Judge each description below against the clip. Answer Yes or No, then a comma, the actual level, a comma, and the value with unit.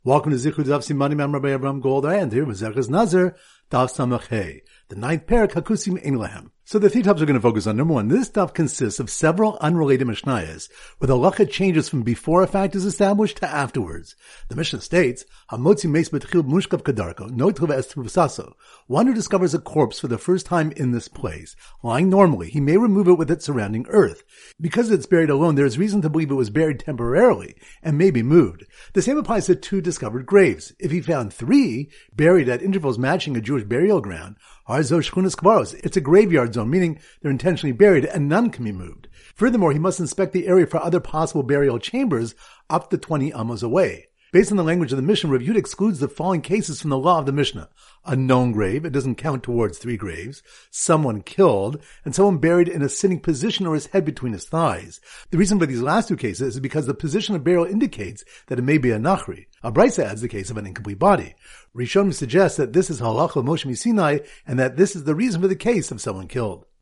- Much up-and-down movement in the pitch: Yes, wide, 6.4 semitones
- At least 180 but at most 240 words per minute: Yes, fast, 205 wpm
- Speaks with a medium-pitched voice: Yes, medium, 155 Hz